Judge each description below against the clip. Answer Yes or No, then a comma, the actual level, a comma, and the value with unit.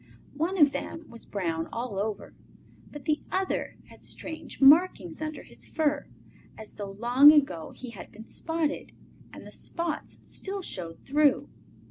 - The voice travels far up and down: Yes, wide, 6.9 semitones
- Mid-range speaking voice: No, very high, 280 Hz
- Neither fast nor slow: Yes, average, 150 wpm